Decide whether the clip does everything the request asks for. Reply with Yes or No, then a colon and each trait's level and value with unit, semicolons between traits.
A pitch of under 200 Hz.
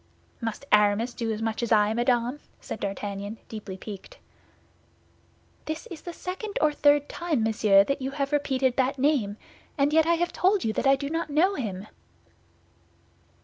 No: very high, 260 Hz